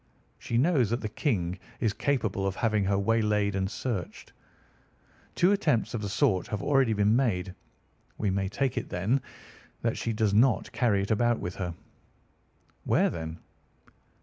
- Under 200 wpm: Yes, average, 160 wpm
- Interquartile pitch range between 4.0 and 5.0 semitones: No, average, 3.6 semitones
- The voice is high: No, low, 105 Hz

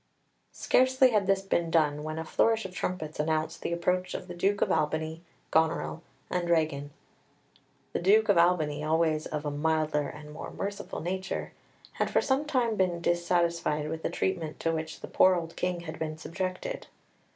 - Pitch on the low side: No, medium, 170 Hz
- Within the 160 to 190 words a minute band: Yes, average, 175 wpm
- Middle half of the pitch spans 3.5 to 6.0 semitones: No, average, 3.1 semitones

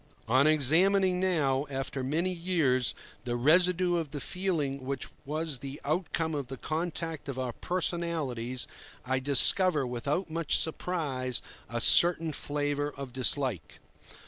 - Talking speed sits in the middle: No, slow, 130 wpm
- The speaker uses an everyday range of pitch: Yes, average, 4.4 semitones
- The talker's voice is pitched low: No, medium, 145 Hz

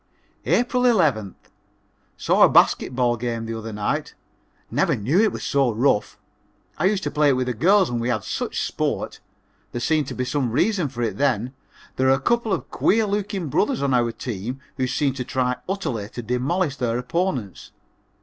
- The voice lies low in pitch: Yes, low, 130 Hz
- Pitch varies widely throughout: Yes, wide, 6.8 semitones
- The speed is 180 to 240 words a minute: Yes, average, 190 wpm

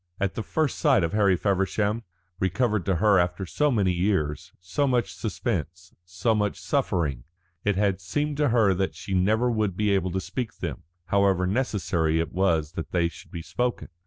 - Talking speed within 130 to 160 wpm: No, average, 185 wpm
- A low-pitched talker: Yes, very low, 95 Hz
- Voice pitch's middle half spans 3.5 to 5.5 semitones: Yes, average, 3.8 semitones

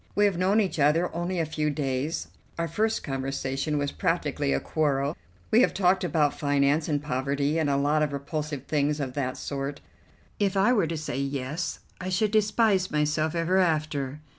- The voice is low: No, medium, 150 Hz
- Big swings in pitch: No, average, 4.1 semitones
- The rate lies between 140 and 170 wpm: No, average, 185 wpm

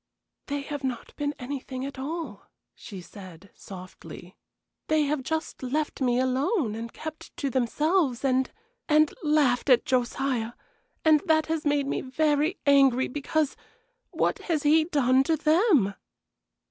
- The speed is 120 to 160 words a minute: Yes, average, 140 wpm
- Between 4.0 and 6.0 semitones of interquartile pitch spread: No, average, 3.5 semitones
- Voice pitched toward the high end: Yes, very high, 280 Hz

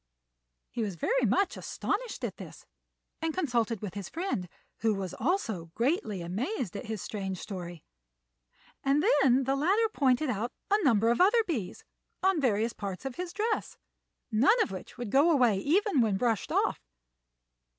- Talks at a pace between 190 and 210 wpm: No, average, 160 wpm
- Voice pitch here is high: Yes, high, 245 Hz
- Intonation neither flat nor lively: No, wide, 8.8 semitones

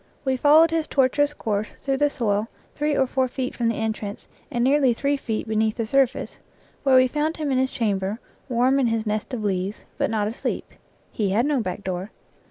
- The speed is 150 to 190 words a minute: No, fast, 205 wpm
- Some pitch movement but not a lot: Yes, average, 4.2 semitones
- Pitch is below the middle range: No, high, 245 Hz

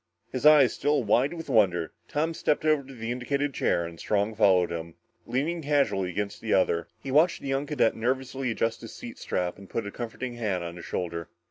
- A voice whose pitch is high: No, low, 120 Hz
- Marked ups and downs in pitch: Yes, wide, 6.7 semitones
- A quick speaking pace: Yes, fast, 210 wpm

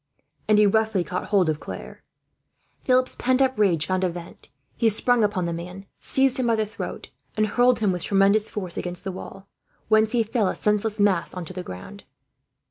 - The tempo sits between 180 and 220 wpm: Yes, fast, 205 wpm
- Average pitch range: Yes, average, 3.5 semitones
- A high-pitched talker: Yes, high, 205 Hz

